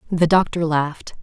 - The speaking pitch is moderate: Yes, medium, 165 Hz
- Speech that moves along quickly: No, average, 145 wpm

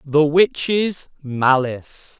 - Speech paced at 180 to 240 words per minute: No, slow, 80 wpm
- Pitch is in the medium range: Yes, medium, 150 Hz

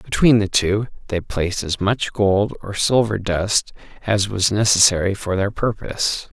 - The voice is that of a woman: No, male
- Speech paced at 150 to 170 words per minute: Yes, average, 160 wpm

